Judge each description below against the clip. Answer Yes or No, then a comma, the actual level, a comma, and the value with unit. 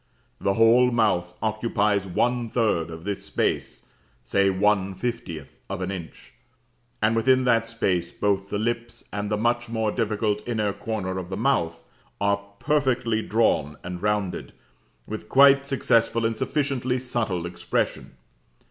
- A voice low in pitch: Yes, low, 110 Hz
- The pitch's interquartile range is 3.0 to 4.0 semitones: Yes, average, 3.5 semitones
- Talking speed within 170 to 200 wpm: No, average, 140 wpm